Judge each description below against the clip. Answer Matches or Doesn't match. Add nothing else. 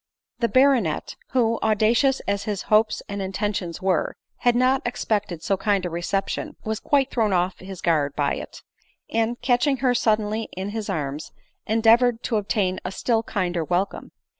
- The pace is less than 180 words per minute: Matches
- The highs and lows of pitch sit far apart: Doesn't match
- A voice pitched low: Doesn't match